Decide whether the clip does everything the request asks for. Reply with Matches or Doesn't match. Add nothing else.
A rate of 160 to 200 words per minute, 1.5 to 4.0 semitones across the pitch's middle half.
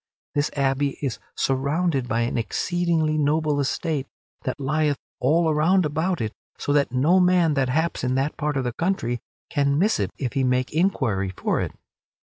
Matches